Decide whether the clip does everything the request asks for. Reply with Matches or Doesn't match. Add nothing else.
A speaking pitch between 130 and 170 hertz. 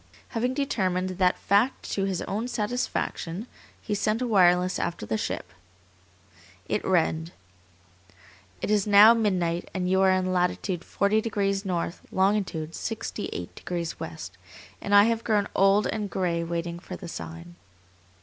Doesn't match